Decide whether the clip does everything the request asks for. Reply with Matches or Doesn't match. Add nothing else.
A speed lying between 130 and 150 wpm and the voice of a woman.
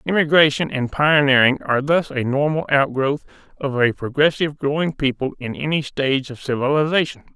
Doesn't match